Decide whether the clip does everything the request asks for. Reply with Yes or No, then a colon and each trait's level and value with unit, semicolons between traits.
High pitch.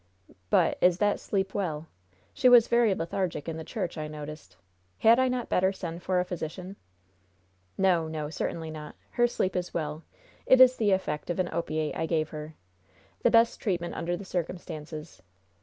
No: medium, 175 Hz